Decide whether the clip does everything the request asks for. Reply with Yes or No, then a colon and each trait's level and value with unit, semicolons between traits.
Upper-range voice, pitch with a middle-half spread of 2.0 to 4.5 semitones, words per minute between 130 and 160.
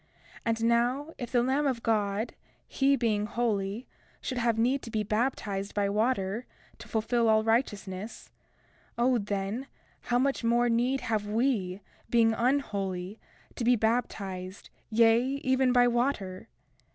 Yes: high, 230 Hz; average, 3.2 semitones; average, 140 wpm